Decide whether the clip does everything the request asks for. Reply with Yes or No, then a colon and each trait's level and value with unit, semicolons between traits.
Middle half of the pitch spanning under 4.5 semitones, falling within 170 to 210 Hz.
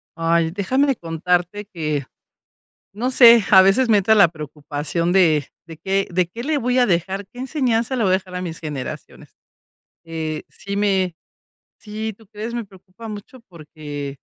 No: average, 5.2 semitones; high, 190 Hz